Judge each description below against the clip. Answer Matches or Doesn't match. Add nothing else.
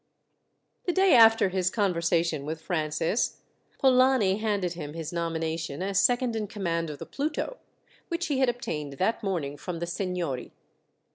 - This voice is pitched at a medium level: Matches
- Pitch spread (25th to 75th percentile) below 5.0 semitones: Doesn't match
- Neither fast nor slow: Matches